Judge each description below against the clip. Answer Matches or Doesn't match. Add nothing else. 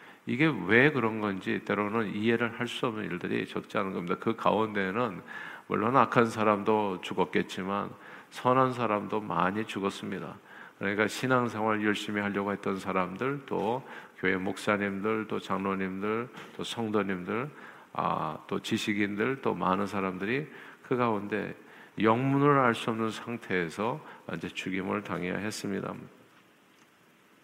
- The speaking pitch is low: Matches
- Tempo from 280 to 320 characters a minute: Matches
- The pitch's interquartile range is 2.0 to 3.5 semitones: Matches